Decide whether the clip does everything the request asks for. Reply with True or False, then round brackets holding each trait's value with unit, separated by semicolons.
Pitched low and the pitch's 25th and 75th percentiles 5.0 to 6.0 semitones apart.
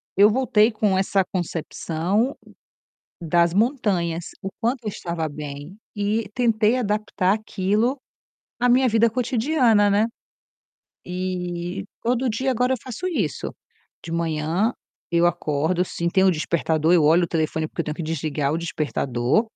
False (190 Hz; 5.4 semitones)